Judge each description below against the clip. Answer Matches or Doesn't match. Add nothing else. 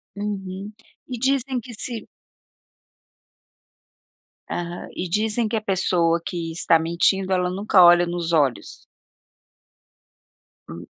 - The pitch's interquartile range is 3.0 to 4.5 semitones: Matches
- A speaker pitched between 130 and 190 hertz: Matches